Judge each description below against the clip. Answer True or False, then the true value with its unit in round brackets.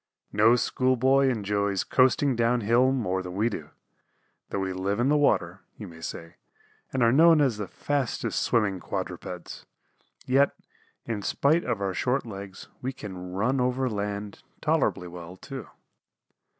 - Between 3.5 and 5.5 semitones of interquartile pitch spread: True (5.1 semitones)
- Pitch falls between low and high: False (110 Hz)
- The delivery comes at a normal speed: True (155 wpm)